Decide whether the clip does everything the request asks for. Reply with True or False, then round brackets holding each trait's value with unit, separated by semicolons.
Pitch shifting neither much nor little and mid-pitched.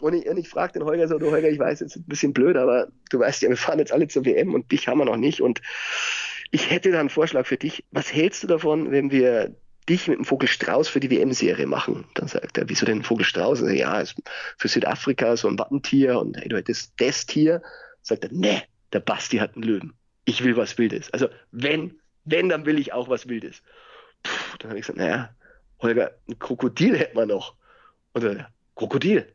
True (3.7 semitones; 155 Hz)